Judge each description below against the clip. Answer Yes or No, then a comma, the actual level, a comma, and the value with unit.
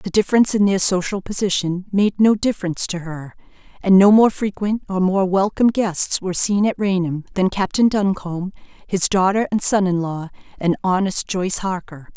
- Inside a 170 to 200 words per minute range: Yes, average, 180 wpm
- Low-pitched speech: No, high, 190 Hz